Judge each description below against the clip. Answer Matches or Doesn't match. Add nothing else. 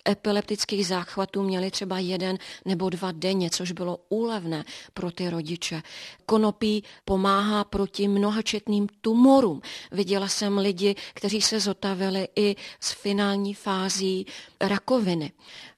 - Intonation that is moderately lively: Doesn't match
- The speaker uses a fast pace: Doesn't match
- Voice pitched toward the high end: Matches